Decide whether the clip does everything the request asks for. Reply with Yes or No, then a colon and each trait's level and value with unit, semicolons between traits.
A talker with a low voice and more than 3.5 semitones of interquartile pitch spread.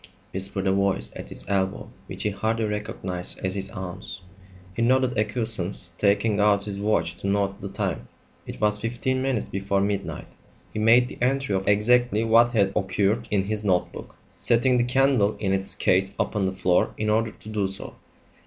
No: low, 105 Hz; average, 2.9 semitones